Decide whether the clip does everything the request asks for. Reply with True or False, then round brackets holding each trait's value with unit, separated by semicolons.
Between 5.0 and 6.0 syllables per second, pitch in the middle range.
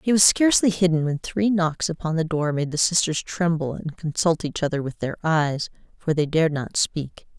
True (5.1 syllables/s; 165 Hz)